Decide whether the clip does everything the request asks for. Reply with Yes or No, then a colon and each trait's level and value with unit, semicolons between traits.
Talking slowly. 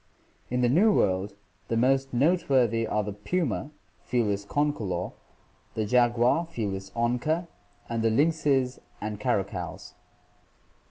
Yes: slow, 115 wpm